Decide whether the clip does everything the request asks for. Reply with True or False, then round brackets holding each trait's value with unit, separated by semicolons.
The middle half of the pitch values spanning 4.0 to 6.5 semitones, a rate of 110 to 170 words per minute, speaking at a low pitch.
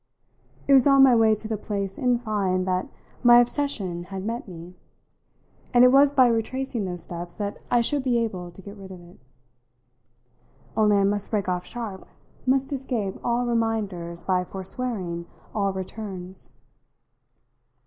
False (4.6 semitones; 160 wpm; 210 Hz)